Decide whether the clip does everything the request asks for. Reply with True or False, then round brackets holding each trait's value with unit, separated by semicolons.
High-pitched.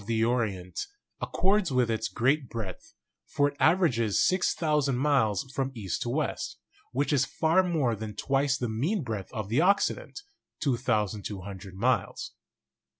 False (125 Hz)